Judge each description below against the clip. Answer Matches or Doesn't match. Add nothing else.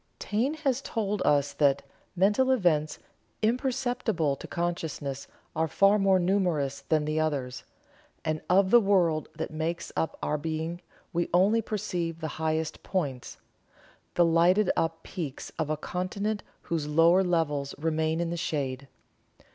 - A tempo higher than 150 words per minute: Doesn't match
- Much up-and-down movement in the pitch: Doesn't match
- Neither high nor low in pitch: Matches